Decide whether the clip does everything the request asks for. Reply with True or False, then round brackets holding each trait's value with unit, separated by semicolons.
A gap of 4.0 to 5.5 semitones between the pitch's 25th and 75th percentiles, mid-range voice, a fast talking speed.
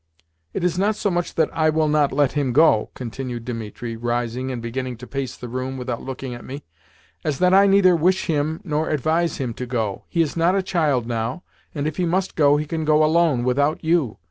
True (4.8 semitones; 145 Hz; 220 wpm)